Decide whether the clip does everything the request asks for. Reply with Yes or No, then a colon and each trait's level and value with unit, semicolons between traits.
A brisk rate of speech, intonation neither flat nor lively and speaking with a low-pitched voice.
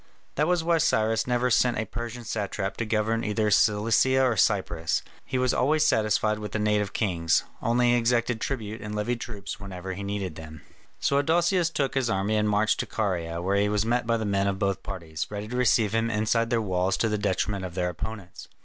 Yes: fast, 210 wpm; average, 3.2 semitones; low, 105 Hz